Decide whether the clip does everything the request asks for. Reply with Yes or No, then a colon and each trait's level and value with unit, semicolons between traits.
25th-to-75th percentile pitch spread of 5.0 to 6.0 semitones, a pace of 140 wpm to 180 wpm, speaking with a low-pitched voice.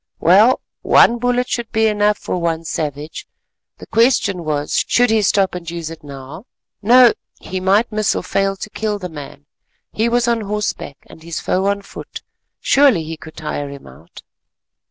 No: wide, 5.4 semitones; average, 175 wpm; high, 195 Hz